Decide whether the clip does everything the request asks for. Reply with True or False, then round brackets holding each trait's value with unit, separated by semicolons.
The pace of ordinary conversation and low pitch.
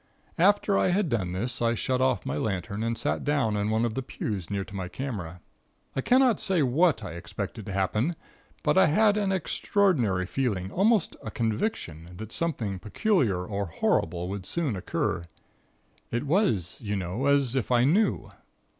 True (175 wpm; 115 Hz)